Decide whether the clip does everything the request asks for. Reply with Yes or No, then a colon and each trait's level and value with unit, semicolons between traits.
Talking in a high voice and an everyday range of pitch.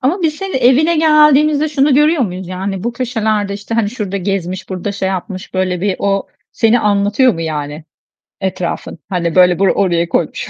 No: high, 200 Hz; wide, 5.9 semitones